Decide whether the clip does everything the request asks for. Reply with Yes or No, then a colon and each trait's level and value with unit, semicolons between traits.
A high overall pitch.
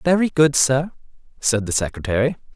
No: low, 135 Hz